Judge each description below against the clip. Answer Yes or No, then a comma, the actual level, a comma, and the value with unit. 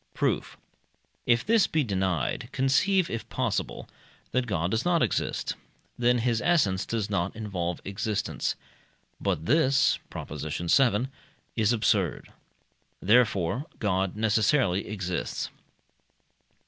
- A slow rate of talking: Yes, slow, 110 wpm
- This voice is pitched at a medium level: No, low, 110 Hz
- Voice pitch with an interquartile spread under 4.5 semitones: No, average, 5.0 semitones